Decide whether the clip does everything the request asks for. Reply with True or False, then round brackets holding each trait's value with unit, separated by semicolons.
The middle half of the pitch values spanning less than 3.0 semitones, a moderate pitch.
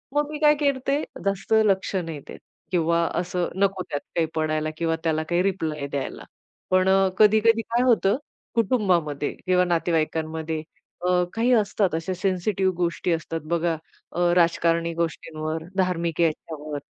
False (3.3 semitones; 175 Hz)